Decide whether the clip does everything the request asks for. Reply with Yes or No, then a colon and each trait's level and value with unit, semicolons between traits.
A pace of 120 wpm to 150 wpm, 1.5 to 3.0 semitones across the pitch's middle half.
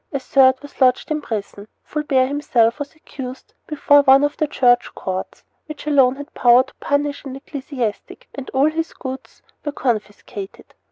No: average, 165 wpm; average, 2.7 semitones